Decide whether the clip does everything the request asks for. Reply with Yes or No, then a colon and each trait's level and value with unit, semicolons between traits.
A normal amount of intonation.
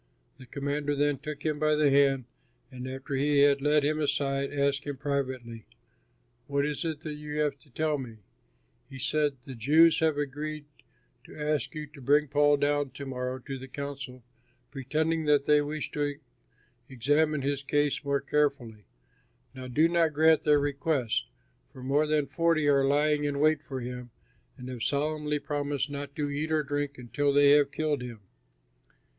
No: narrow, 1.7 semitones